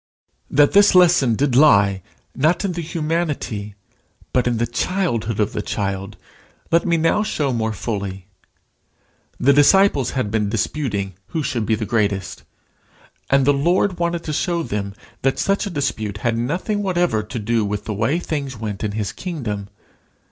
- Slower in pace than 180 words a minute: Yes, average, 165 wpm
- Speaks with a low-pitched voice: Yes, low, 125 Hz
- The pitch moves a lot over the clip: Yes, wide, 7.7 semitones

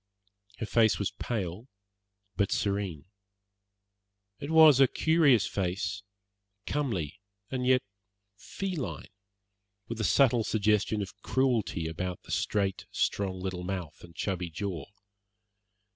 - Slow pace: Yes, slow, 115 wpm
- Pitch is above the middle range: No, low, 100 Hz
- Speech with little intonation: No, average, 5.3 semitones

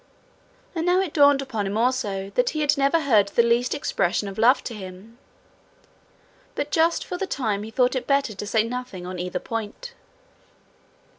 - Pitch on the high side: Yes, high, 235 Hz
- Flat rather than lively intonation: No, wide, 5.5 semitones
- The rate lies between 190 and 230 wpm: No, average, 180 wpm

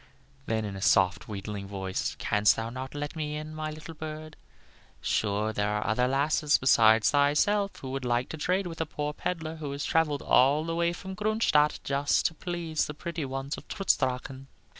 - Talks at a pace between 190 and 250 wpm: Yes, average, 195 wpm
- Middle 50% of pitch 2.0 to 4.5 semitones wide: No, average, 4.9 semitones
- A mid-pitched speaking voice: Yes, medium, 145 Hz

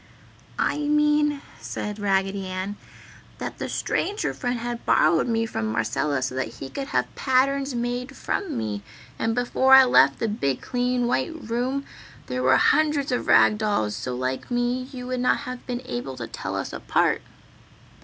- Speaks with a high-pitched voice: Yes, high, 240 Hz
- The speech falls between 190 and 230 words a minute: No, average, 170 wpm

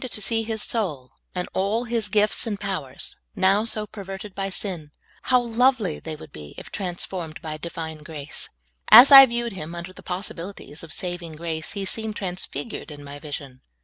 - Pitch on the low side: No, high, 190 Hz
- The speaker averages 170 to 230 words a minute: Yes, average, 190 wpm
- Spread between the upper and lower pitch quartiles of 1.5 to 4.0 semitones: No, average, 5.2 semitones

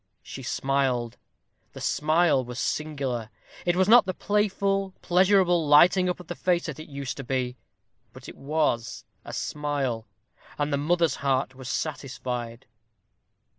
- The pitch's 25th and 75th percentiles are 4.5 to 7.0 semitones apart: Yes, average, 5.2 semitones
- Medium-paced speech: Yes, average, 145 wpm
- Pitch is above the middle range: No, medium, 145 Hz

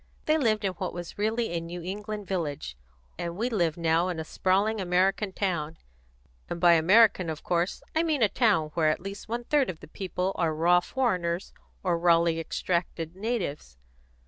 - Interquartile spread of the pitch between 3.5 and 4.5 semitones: Yes, average, 3.8 semitones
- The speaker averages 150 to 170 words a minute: No, average, 180 wpm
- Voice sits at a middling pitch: Yes, medium, 180 Hz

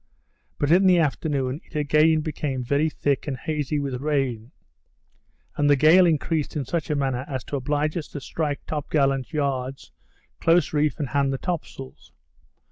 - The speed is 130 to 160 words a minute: No, average, 175 wpm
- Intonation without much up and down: Yes, narrow, 2.3 semitones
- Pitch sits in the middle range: Yes, medium, 145 Hz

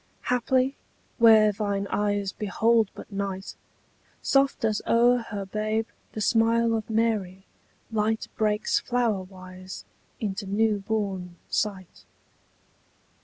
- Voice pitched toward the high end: Yes, high, 215 Hz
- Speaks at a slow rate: Yes, slow, 105 wpm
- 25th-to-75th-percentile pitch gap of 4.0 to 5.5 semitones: No, narrow, 2.4 semitones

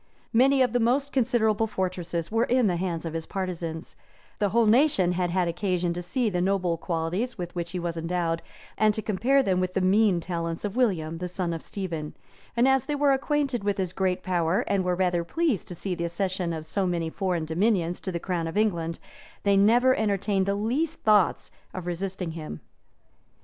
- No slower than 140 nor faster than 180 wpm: No, fast, 205 wpm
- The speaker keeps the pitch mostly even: No, average, 4.2 semitones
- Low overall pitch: No, medium, 185 Hz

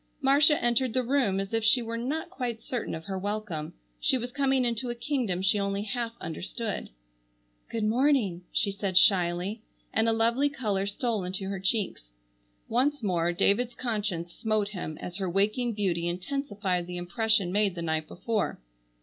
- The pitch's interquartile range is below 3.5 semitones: No, average, 4.4 semitones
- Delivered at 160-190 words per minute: Yes, average, 170 wpm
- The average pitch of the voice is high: Yes, high, 215 Hz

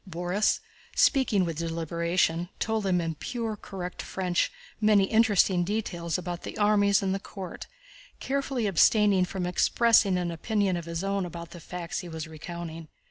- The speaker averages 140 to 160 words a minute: Yes, average, 155 wpm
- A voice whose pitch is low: No, medium, 180 Hz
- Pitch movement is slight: No, average, 3.4 semitones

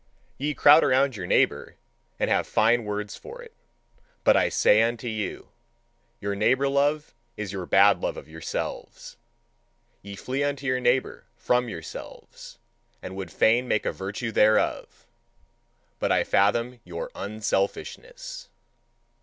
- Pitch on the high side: No, low, 115 Hz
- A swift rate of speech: No, slow, 135 wpm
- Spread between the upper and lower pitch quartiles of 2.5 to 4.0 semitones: No, average, 5.3 semitones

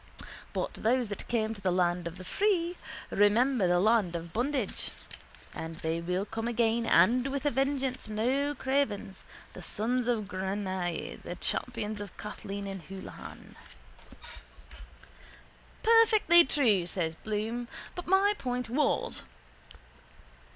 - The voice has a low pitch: No, high, 220 Hz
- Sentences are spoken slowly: Yes, slow, 130 wpm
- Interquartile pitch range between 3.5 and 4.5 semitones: No, wide, 5.6 semitones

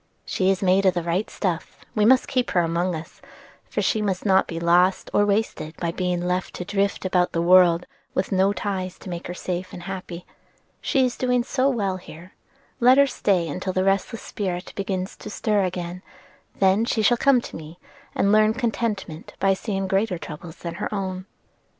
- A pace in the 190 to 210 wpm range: Yes, average, 200 wpm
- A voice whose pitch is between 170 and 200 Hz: Yes, high, 190 Hz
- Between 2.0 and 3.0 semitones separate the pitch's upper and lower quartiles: Yes, average, 2.7 semitones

